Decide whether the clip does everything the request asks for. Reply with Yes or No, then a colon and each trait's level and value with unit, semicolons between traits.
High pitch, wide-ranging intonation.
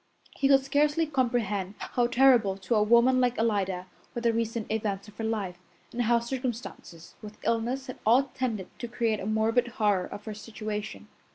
No: high, 225 Hz; average, 2.9 semitones